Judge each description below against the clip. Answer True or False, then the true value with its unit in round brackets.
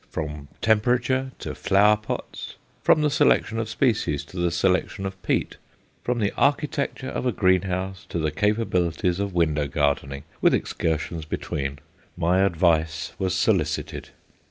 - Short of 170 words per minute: True (140 wpm)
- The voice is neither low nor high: False (95 Hz)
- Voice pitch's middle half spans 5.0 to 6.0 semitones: True (5.3 semitones)